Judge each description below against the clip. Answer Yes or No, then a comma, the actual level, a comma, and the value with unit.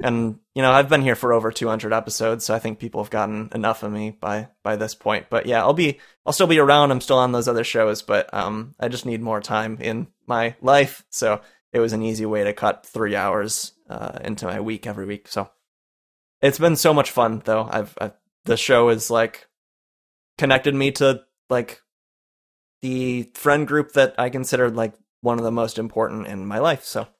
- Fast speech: Yes, fast, 210 wpm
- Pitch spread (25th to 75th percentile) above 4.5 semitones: No, average, 3.4 semitones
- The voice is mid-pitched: No, low, 115 Hz